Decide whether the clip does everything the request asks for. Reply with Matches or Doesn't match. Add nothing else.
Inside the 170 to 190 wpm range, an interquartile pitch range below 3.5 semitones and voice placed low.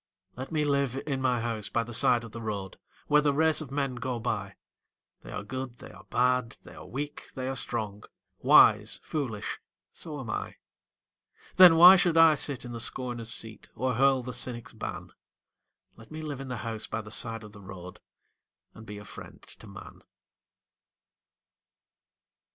Doesn't match